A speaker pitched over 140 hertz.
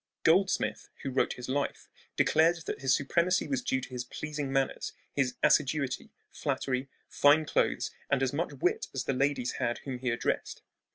No: low, 135 Hz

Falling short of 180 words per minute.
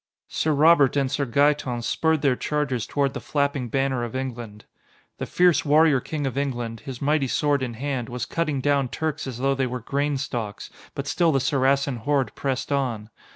No: average, 190 wpm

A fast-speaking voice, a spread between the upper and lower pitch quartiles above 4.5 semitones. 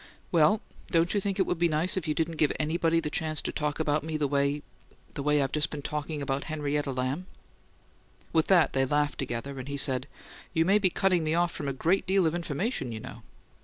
No: fast, 230 wpm; average, 3.1 semitones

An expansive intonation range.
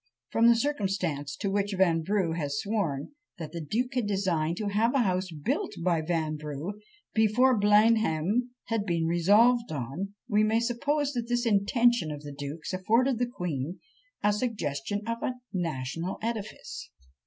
Yes: wide, 6.0 semitones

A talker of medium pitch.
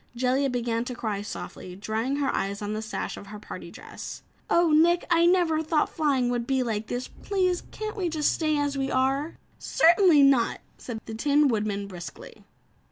No: very high, 265 Hz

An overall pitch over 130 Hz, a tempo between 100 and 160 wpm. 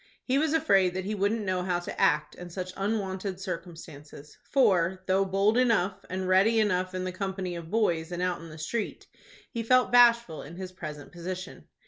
No: medium, 185 Hz; average, 190 wpm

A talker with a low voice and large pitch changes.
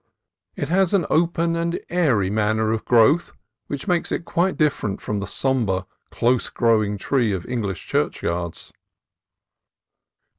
Yes: low, 120 Hz; wide, 8.2 semitones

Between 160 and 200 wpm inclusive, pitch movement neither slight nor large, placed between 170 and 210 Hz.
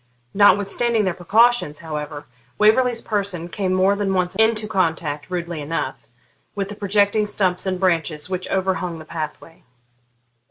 No: slow, 135 wpm; average, 3.7 semitones; medium, 185 Hz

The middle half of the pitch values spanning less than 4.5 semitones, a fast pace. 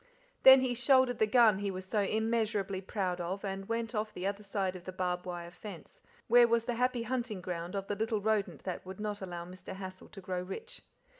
Yes: average, 3.5 semitones; fast, 220 wpm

